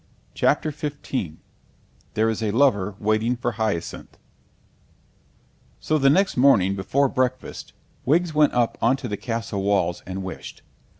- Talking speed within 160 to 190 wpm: No, slow, 135 wpm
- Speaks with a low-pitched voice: Yes, low, 115 Hz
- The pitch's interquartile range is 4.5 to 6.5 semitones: Yes, average, 5.2 semitones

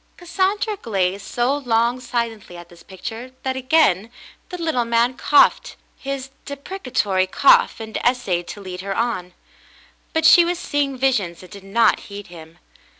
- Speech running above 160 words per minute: No, average, 150 wpm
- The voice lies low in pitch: No, high, 235 Hz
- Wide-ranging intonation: Yes, wide, 6.1 semitones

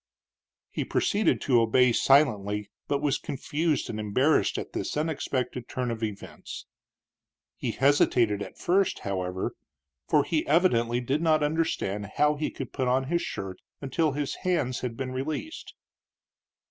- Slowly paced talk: No, average, 145 wpm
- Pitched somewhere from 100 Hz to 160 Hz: Yes, low, 135 Hz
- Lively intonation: No, average, 4.7 semitones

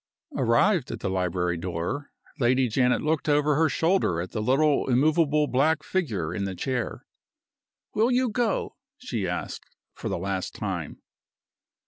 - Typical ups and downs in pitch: No, wide, 8.5 semitones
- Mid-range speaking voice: No, low, 130 Hz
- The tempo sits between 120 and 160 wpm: Yes, average, 145 wpm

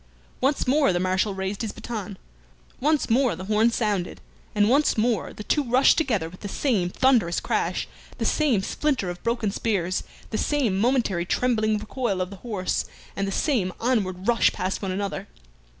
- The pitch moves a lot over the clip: No, average, 4.7 semitones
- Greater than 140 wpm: Yes, average, 175 wpm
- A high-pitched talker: Yes, high, 215 Hz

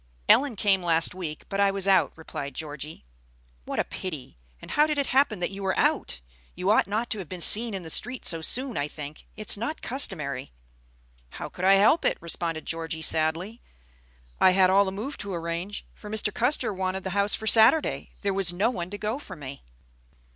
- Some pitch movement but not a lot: Yes, average, 4.6 semitones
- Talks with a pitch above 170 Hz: Yes, high, 190 Hz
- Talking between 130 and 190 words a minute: No, fast, 205 wpm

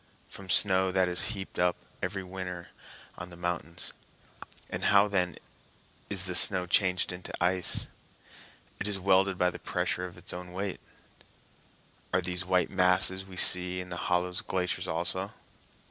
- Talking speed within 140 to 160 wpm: Yes, average, 155 wpm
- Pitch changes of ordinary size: No, narrow, 1.0 semitones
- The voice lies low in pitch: Yes, very low, 90 Hz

